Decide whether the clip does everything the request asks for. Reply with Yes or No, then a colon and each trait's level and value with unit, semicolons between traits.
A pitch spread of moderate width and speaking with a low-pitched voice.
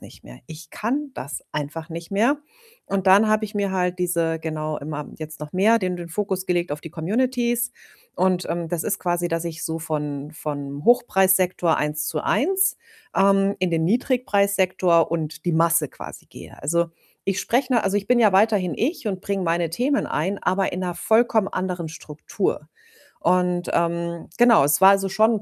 No: average, 3.9 semitones; medium, 180 Hz